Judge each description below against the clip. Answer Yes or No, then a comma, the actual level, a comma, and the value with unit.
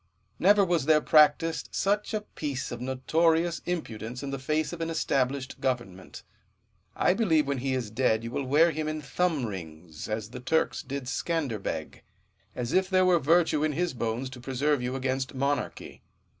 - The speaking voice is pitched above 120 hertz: Yes, medium, 140 Hz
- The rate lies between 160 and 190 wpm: Yes, average, 175 wpm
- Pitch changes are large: No, average, 4.6 semitones